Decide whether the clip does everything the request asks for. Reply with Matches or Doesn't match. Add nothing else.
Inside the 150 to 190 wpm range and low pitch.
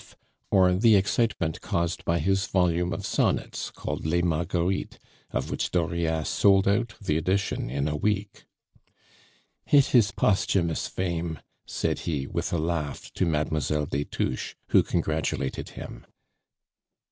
Doesn't match